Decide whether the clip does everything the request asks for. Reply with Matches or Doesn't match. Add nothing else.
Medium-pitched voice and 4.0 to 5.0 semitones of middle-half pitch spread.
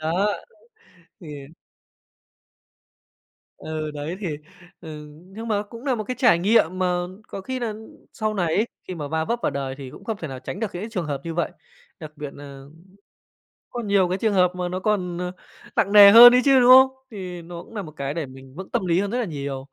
Doesn't match